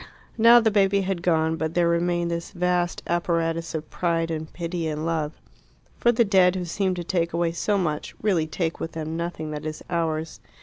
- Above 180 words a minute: Yes, average, 200 wpm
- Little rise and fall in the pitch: Yes, narrow, 2.0 semitones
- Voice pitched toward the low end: No, medium, 170 Hz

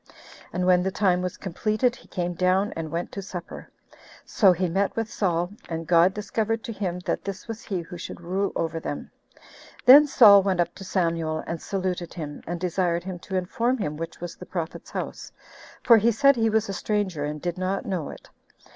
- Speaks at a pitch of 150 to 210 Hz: Yes, medium, 185 Hz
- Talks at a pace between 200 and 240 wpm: Yes, fast, 205 wpm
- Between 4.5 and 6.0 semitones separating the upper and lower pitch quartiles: No, average, 3.1 semitones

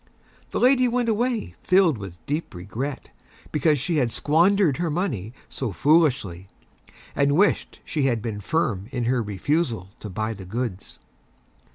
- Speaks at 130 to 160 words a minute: Yes, average, 150 wpm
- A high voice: No, low, 135 Hz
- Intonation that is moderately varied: No, wide, 8.0 semitones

